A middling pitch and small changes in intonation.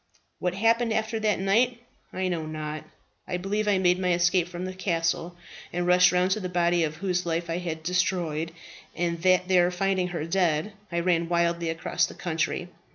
Yes: medium, 180 Hz; narrow, 1.8 semitones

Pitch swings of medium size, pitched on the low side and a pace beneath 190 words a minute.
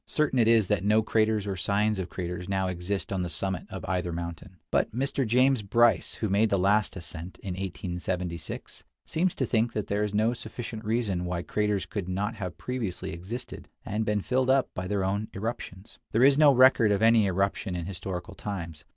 No: average, 3.5 semitones; low, 100 Hz; average, 200 wpm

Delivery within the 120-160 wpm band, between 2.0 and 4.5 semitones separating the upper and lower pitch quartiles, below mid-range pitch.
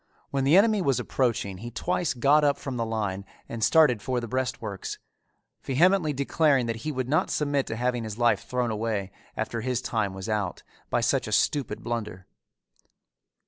No: average, 180 wpm; average, 4.1 semitones; low, 120 Hz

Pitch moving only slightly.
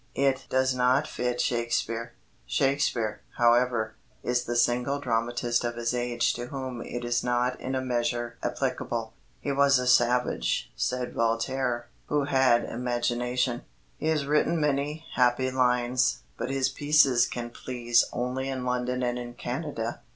Yes: narrow, 1.6 semitones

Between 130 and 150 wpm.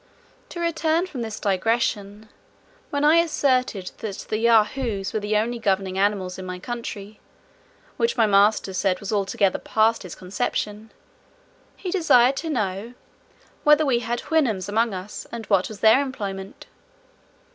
Yes: average, 145 wpm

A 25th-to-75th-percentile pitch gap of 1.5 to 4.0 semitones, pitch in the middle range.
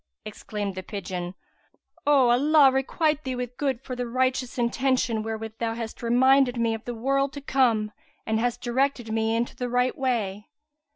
No: average, 3.0 semitones; high, 245 Hz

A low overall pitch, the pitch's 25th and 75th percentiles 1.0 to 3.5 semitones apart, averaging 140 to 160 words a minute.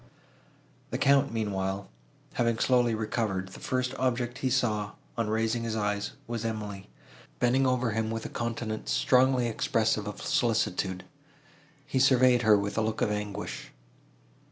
Yes: low, 115 Hz; average, 3.0 semitones; average, 145 wpm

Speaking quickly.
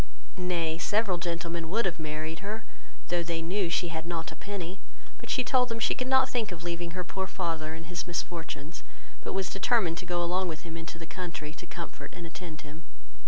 Yes: fast, 210 wpm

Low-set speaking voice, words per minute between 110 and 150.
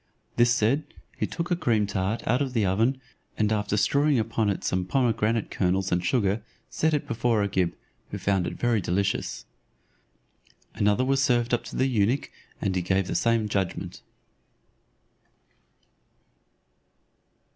Yes: low, 110 Hz; average, 145 wpm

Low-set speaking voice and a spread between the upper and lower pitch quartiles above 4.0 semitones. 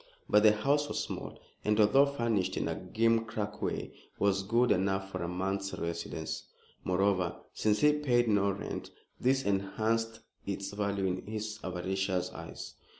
No: low, 105 Hz; average, 2.8 semitones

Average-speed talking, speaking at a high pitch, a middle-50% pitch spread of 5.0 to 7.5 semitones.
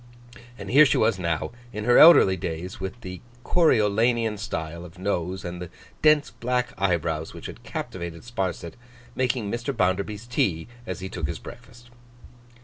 No: average, 155 wpm; low, 100 Hz; average, 5.3 semitones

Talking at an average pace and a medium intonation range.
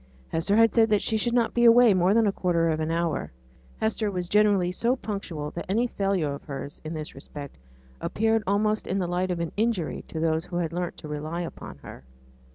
No: fast, 225 wpm; average, 4.7 semitones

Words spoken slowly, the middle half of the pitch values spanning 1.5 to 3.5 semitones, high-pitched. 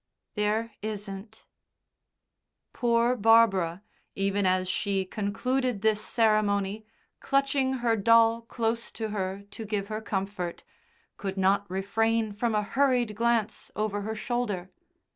Yes: slow, 120 wpm; narrow, 2.6 semitones; high, 215 Hz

